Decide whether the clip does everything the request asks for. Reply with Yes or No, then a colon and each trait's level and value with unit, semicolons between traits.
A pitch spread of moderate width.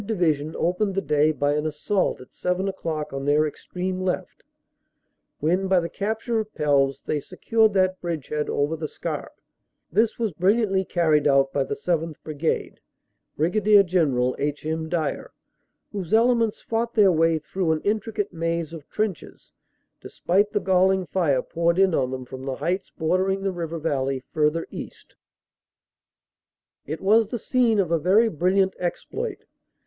Yes: average, 4.4 semitones